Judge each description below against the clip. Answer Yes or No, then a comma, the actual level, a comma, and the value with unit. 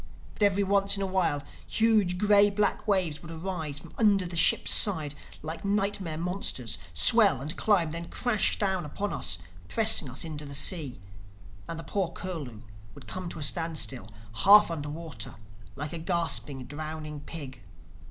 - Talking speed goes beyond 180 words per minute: No, average, 165 wpm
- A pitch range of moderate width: Yes, average, 4.9 semitones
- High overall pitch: No, medium, 170 Hz